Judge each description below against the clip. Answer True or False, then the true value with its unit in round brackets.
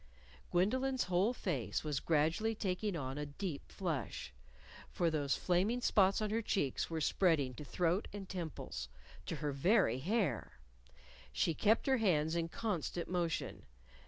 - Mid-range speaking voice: True (175 Hz)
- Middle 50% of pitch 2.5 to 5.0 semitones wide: False (5.4 semitones)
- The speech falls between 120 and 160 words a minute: True (145 wpm)